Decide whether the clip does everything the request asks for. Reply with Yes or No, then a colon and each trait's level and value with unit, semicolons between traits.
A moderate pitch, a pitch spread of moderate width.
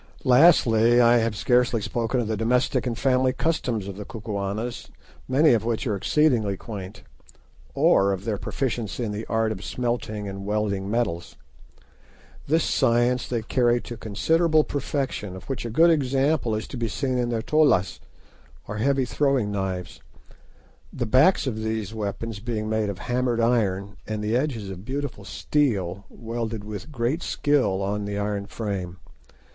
No: low, 115 Hz; average, 3.6 semitones